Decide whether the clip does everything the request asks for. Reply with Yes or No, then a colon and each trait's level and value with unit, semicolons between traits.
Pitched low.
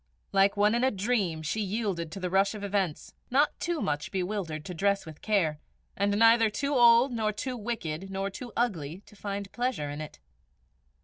No: high, 200 Hz